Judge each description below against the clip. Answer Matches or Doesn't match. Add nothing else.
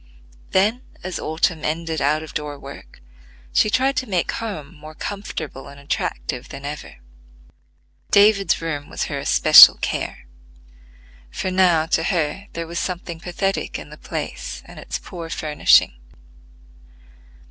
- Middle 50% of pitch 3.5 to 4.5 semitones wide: Matches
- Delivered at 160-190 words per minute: Doesn't match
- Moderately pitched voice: Matches